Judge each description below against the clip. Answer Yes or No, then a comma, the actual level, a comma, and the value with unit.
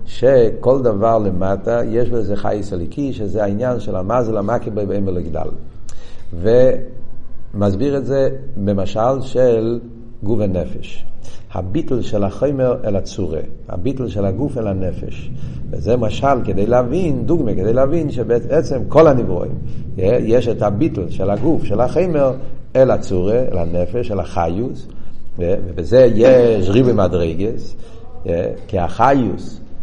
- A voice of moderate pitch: No, low, 115 Hz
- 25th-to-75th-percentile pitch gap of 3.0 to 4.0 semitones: No, average, 4.4 semitones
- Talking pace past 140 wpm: No, average, 125 wpm